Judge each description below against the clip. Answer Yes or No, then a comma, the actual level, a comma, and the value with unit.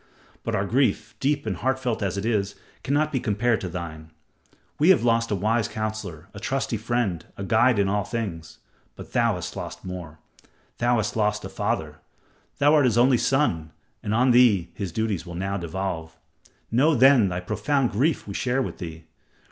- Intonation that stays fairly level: No, average, 4.6 semitones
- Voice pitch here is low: Yes, low, 110 Hz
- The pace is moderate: Yes, average, 190 wpm